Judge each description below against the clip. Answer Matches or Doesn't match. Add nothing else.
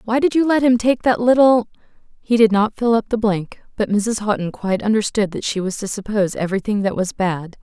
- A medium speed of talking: Doesn't match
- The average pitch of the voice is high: Matches